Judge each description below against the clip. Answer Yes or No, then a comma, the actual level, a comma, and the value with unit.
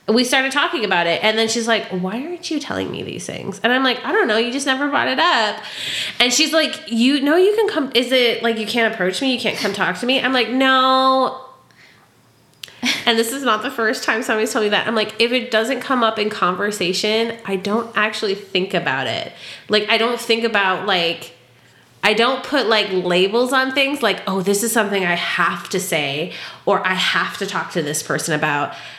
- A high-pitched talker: Yes, high, 225 Hz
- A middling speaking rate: No, fast, 225 wpm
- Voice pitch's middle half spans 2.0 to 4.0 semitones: No, average, 4.8 semitones